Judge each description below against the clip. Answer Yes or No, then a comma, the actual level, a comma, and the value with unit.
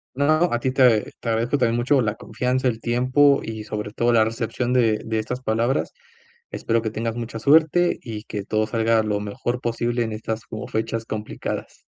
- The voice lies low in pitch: Yes, low, 115 Hz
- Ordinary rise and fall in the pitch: No, narrow, 2.2 semitones